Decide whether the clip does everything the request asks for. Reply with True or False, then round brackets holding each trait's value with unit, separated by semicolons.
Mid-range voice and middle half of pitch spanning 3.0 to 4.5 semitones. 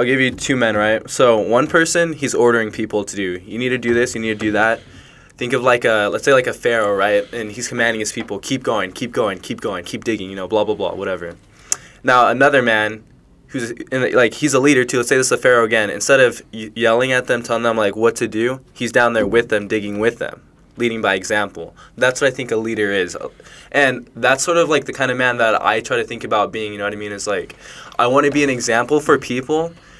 False (115 Hz; 3.3 semitones)